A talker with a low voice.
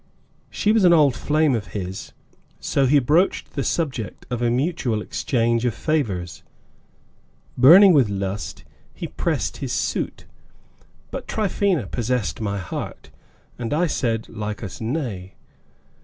Yes: low, 125 Hz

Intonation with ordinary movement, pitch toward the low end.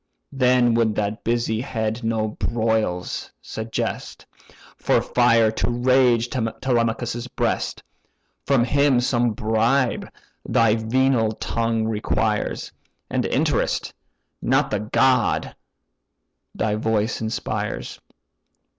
No: narrow, 2.0 semitones; low, 115 Hz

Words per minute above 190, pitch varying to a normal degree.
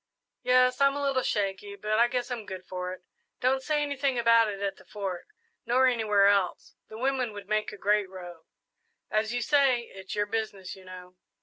Yes: average, 200 wpm; average, 4.4 semitones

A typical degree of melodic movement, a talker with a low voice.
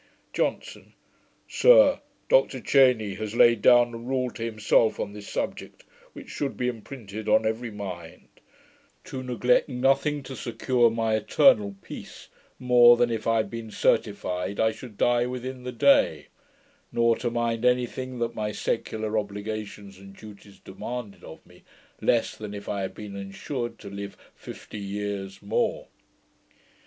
Yes: average, 3.3 semitones; low, 115 Hz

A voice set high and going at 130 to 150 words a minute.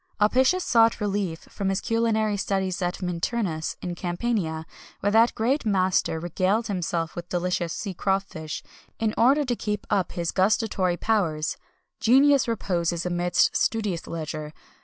Yes: high, 195 Hz; average, 140 wpm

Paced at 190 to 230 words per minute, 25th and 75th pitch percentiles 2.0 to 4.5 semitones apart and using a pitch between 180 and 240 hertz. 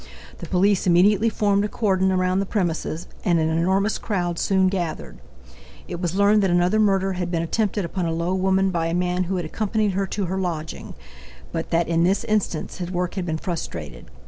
Yes: average, 200 wpm; narrow, 2.5 semitones; medium, 185 Hz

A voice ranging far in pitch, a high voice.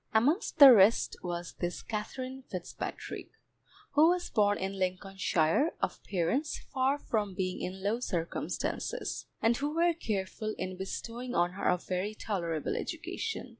Yes: wide, 5.9 semitones; high, 205 Hz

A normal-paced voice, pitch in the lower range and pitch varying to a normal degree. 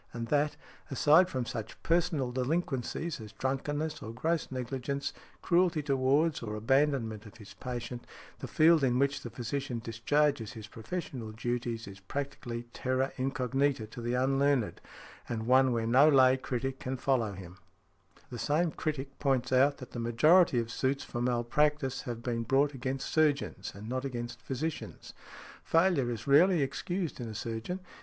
Yes: average, 155 wpm; low, 130 Hz; average, 3.5 semitones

